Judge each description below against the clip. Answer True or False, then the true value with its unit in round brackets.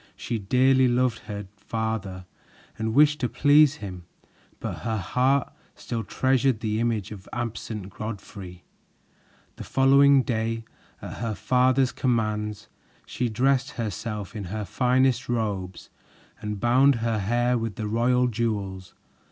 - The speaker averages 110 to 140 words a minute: True (135 wpm)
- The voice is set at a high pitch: False (115 Hz)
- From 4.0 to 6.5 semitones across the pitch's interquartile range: False (3.2 semitones)